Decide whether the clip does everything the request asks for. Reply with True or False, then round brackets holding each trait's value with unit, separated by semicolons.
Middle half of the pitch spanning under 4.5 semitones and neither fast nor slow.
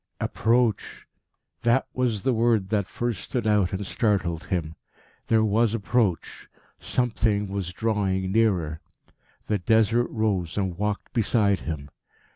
False (3.2 semitones; 125 wpm)